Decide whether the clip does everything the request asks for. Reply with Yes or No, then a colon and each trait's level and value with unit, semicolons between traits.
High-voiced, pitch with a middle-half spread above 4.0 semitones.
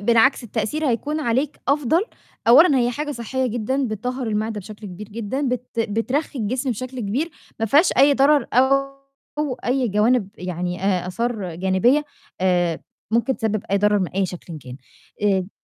Yes: high, 230 Hz; average, 4.8 semitones